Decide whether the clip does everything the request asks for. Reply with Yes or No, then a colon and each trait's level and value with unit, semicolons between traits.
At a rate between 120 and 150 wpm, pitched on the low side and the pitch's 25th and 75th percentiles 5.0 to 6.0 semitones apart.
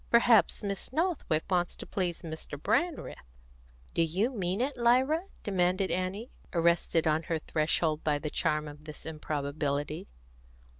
No: average, 140 wpm; medium, 175 Hz; wide, 5.6 semitones